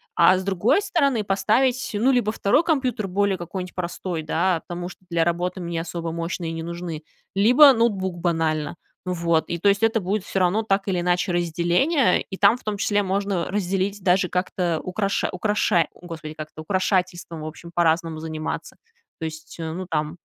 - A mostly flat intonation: No, average, 3.2 semitones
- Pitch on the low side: No, medium, 180 Hz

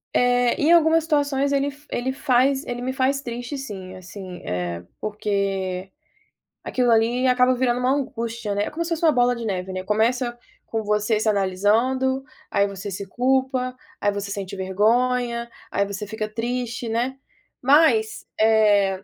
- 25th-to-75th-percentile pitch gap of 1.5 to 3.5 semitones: No, average, 4.3 semitones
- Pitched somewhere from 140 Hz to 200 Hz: No, high, 235 Hz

